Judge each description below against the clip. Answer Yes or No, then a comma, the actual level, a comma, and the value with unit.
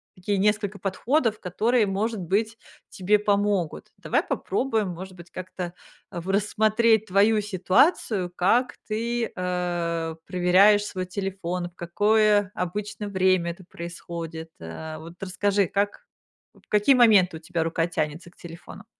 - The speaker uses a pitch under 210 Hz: Yes, high, 190 Hz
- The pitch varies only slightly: No, average, 3.2 semitones